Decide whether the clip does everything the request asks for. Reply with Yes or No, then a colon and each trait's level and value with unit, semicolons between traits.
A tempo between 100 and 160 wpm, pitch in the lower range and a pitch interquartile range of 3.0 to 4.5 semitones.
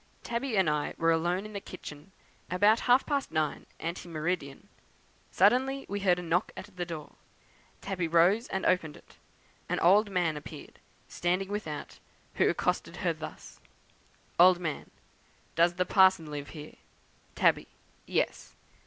No: average, 145 wpm; medium, 180 Hz; average, 3.6 semitones